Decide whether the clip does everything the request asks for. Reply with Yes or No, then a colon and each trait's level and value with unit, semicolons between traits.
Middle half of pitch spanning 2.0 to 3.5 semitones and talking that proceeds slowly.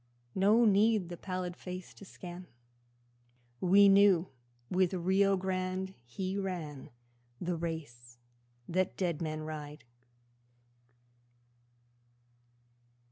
Yes: narrow, 2.6 semitones; slow, 90 wpm